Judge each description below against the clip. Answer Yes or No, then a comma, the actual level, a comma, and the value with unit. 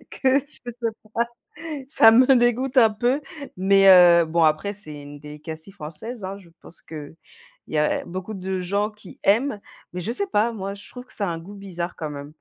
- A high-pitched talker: Yes, high, 195 Hz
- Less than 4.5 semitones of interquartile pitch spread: No, average, 5.2 semitones